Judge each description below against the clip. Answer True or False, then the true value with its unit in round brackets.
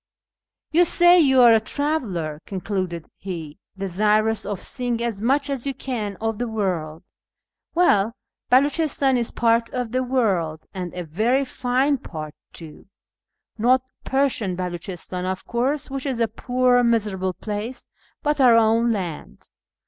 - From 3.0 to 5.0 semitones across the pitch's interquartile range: False (5.4 semitones)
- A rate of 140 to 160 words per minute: True (150 wpm)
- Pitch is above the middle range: True (230 Hz)